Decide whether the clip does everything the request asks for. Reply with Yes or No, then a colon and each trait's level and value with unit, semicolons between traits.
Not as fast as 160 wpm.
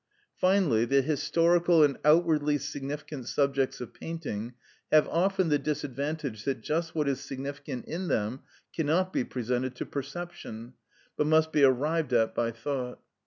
Yes: average, 145 wpm